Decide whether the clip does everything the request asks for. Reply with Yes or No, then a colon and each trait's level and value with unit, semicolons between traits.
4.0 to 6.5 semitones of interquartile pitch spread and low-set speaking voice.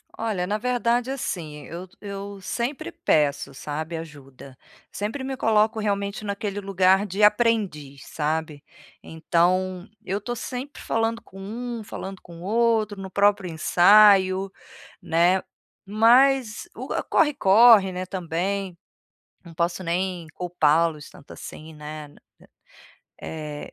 No: average, 4.4 semitones; high, 190 Hz